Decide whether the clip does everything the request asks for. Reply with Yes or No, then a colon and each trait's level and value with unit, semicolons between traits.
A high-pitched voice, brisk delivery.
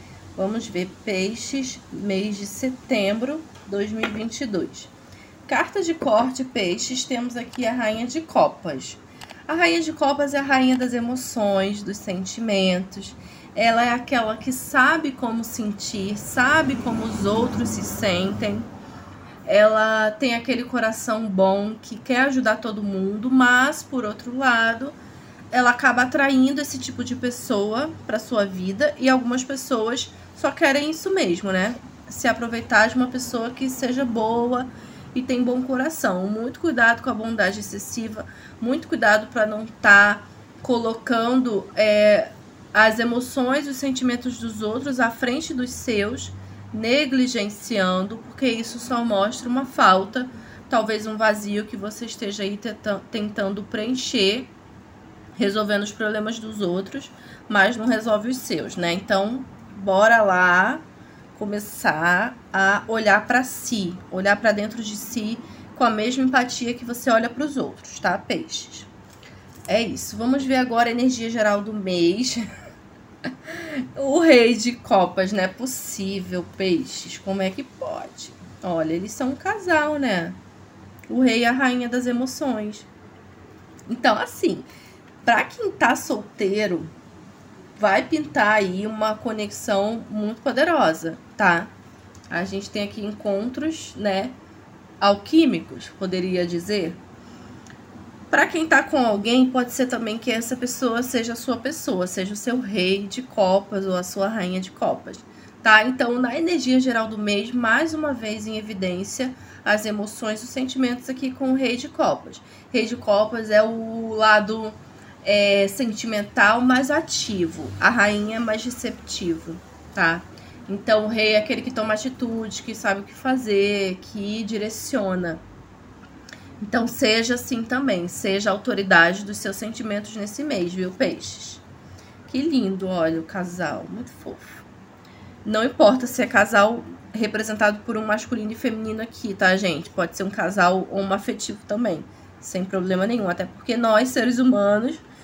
No: high, 225 Hz; average, 145 wpm